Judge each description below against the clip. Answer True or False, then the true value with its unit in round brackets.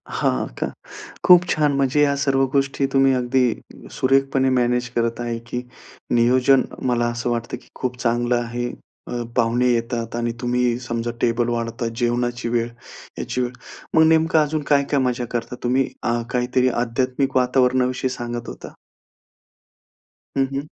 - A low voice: True (125 Hz)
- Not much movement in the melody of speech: True (2.0 semitones)